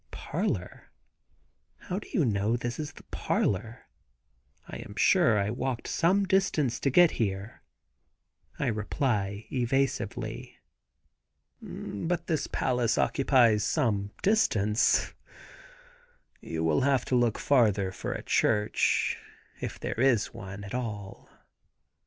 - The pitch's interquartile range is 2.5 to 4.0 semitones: No, average, 5.0 semitones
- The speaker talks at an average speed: No, slow, 115 wpm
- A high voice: No, low, 120 Hz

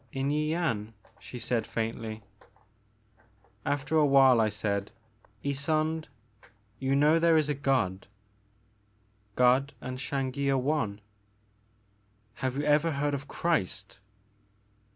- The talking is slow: Yes, slow, 120 wpm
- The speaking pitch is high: No, low, 135 Hz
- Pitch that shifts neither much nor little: Yes, average, 4.9 semitones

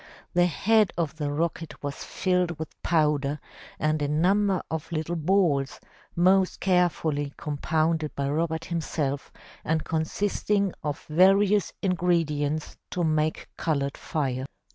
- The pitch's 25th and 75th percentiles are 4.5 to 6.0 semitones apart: No, average, 3.1 semitones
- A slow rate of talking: Yes, slow, 120 wpm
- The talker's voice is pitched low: No, medium, 160 Hz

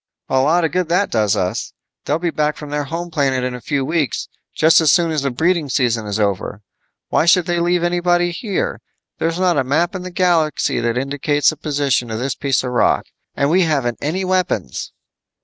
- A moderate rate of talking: No, fast, 210 wpm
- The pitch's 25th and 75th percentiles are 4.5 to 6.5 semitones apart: Yes, average, 4.8 semitones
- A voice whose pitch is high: No, medium, 150 Hz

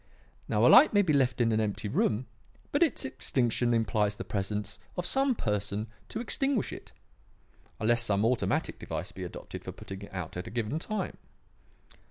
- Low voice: Yes, low, 110 Hz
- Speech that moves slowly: No, average, 180 wpm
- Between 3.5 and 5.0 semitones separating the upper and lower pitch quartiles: Yes, average, 4.3 semitones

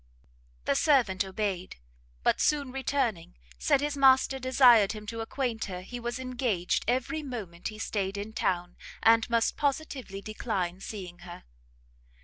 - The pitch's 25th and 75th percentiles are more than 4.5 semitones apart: Yes, average, 5.2 semitones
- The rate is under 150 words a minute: Yes, average, 140 wpm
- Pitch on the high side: Yes, high, 225 Hz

